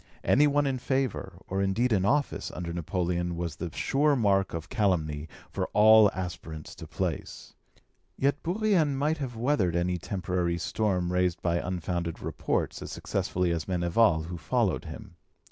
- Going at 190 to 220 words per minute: No, average, 155 wpm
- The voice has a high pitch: No, very low, 95 Hz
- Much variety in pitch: Yes, wide, 6.5 semitones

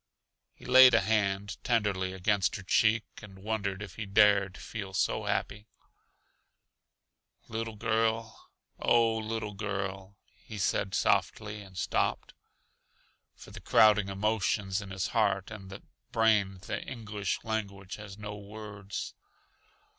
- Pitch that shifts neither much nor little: No, narrow, 2.1 semitones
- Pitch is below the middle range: Yes, low, 105 Hz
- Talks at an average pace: No, slow, 125 wpm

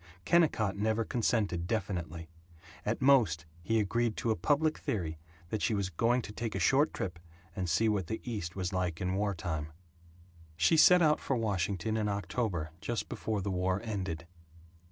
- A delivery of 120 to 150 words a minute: No, average, 170 wpm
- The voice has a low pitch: Yes, low, 100 Hz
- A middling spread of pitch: Yes, average, 4.3 semitones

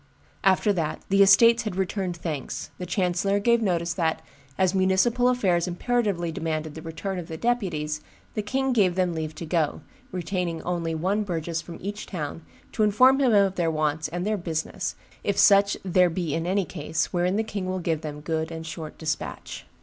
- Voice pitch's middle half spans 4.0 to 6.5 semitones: No, average, 3.6 semitones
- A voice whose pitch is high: No, medium, 180 Hz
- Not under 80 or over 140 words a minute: No, average, 190 wpm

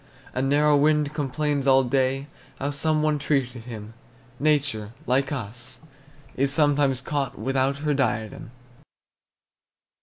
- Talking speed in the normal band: No, slow, 120 wpm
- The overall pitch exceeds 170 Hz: No, low, 135 Hz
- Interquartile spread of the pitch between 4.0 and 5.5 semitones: No, narrow, 2.4 semitones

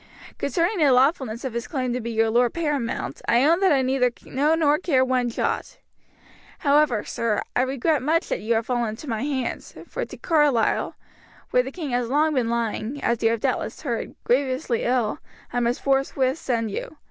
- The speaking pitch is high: Yes, very high, 255 Hz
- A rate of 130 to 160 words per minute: No, average, 195 wpm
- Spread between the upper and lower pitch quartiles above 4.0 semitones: No, average, 3.7 semitones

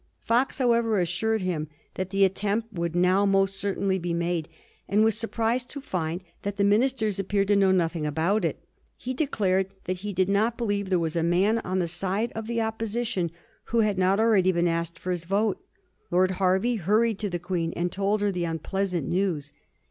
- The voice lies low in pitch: No, high, 195 Hz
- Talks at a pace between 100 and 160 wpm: No, average, 200 wpm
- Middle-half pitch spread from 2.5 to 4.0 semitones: Yes, average, 3.5 semitones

